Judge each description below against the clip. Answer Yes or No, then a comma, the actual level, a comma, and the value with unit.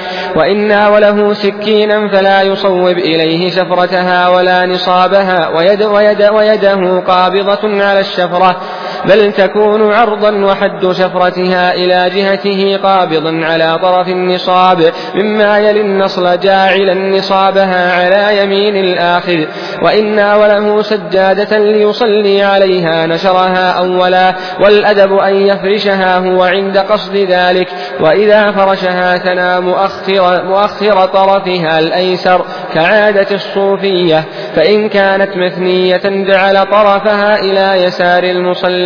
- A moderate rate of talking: Yes, average, 100 wpm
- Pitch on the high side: Yes, high, 195 Hz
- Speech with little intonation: Yes, narrow, 1.7 semitones